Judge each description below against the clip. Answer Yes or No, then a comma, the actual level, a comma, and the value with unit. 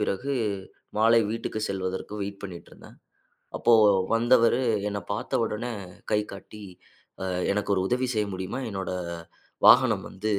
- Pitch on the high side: No, low, 105 Hz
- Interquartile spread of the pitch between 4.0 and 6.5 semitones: No, average, 2.8 semitones